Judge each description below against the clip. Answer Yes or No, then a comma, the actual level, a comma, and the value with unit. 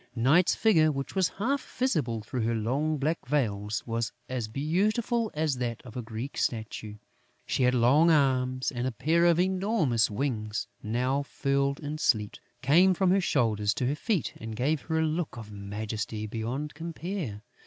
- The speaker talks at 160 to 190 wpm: Yes, average, 170 wpm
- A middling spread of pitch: No, wide, 6.1 semitones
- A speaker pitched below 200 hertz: Yes, low, 135 Hz